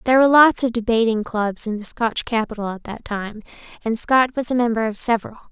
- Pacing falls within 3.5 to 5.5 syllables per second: No, 5.9 syllables/s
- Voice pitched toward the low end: No, high, 230 Hz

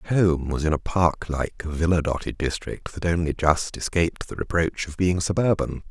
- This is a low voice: Yes, very low, 85 Hz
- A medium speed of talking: Yes, average, 195 wpm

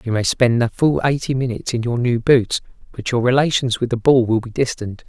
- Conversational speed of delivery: No, fast, 235 wpm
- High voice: No, low, 120 Hz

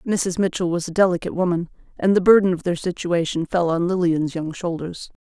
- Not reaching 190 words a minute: No, average, 195 wpm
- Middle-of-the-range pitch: Yes, medium, 175 Hz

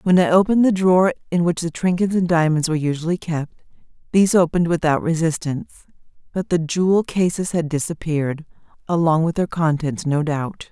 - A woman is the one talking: Yes, female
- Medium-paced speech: Yes, average, 170 wpm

